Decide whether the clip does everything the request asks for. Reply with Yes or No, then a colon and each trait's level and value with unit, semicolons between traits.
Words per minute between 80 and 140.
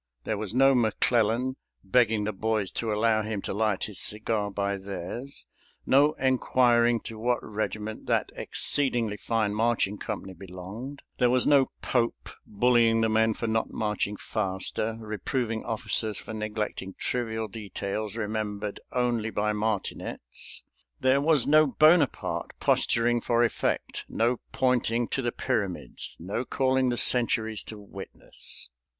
Yes: slow, 135 wpm